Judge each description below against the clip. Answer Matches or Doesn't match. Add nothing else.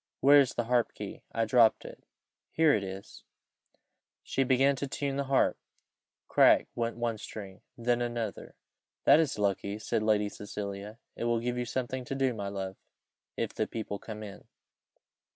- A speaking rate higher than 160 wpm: Matches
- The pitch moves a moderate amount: Matches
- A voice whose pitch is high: Doesn't match